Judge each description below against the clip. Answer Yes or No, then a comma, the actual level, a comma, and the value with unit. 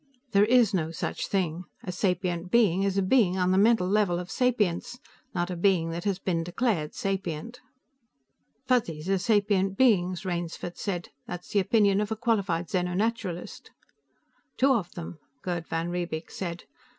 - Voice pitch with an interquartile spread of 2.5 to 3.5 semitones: Yes, average, 3.1 semitones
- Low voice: No, medium, 185 Hz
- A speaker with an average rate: Yes, average, 160 wpm